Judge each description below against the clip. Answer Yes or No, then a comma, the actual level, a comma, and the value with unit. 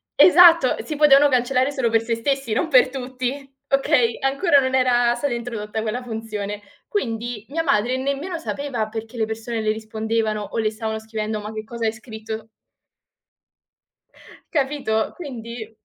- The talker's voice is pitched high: Yes, high, 235 Hz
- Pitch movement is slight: No, average, 3.6 semitones